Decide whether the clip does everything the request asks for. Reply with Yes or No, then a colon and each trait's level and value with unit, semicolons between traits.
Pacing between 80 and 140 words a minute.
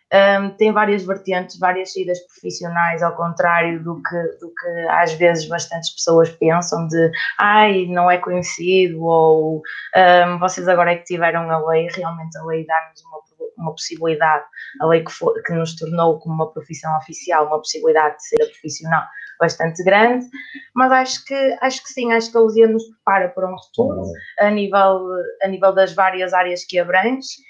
No: average, 175 wpm